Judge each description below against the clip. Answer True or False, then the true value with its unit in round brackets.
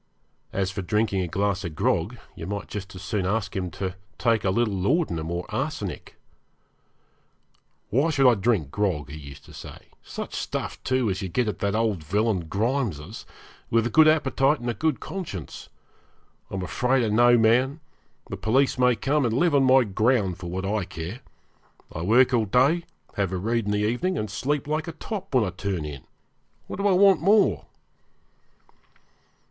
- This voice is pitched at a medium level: False (110 Hz)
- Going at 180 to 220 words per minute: True (185 wpm)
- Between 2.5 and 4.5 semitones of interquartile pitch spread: False (5.6 semitones)